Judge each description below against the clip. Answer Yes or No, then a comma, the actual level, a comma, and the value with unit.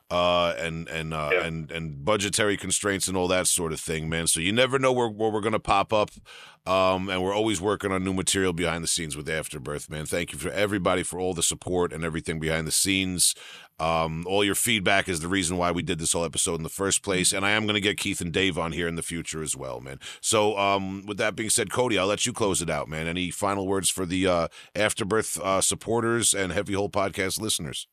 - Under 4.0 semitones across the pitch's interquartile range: Yes, average, 3.2 semitones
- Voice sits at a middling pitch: No, very low, 95 Hz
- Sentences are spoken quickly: Yes, fast, 245 wpm